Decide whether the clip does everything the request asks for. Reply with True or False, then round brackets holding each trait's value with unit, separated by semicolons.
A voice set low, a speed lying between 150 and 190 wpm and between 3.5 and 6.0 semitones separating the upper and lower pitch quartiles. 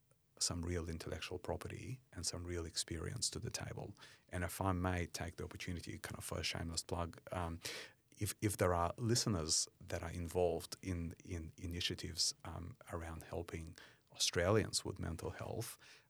True (90 Hz; 160 wpm; 4.2 semitones)